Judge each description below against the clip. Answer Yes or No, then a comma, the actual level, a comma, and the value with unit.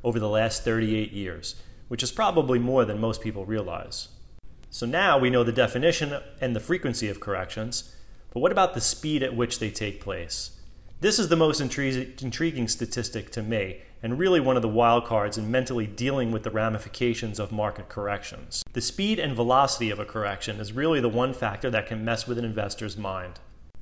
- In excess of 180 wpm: Yes, average, 195 wpm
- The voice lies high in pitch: No, low, 115 Hz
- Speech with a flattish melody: No, average, 3.2 semitones